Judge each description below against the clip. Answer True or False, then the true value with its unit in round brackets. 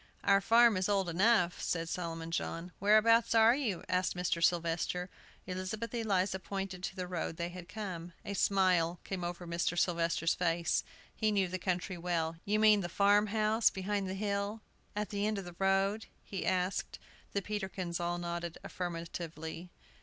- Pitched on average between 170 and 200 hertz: True (185 Hz)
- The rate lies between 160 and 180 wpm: True (170 wpm)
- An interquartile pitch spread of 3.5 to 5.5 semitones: False (2.9 semitones)